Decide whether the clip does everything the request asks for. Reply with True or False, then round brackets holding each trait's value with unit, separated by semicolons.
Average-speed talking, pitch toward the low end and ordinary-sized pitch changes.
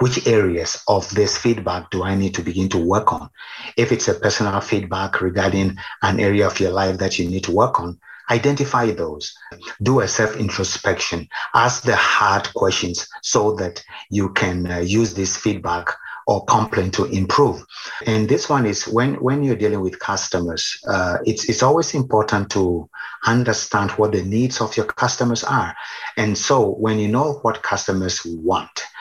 True (175 wpm; 105 Hz; 3.6 semitones)